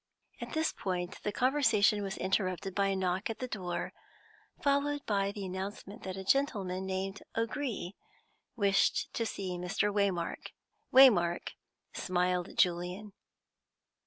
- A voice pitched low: No, high, 195 Hz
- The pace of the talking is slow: Yes, slow, 130 wpm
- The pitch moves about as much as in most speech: Yes, average, 3.2 semitones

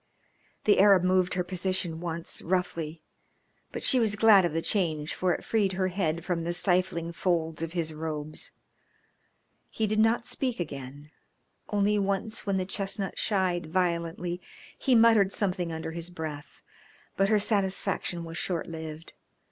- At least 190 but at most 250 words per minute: No, average, 155 wpm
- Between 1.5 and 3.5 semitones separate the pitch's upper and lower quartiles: Yes, average, 3.2 semitones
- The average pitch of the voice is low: No, medium, 180 Hz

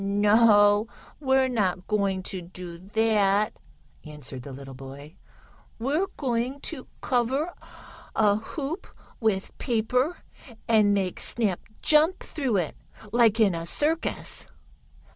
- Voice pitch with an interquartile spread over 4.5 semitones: Yes, average, 5.1 semitones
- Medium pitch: No, high, 215 Hz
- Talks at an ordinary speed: No, slow, 115 wpm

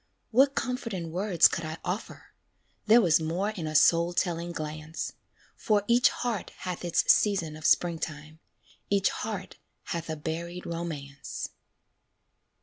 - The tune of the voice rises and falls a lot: No, average, 4.0 semitones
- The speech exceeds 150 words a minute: No, average, 140 wpm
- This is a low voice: No, medium, 170 Hz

